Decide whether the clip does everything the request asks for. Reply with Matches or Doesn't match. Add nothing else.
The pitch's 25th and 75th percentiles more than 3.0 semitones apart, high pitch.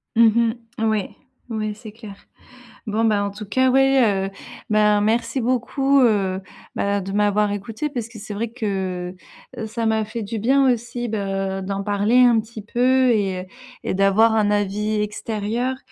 Doesn't match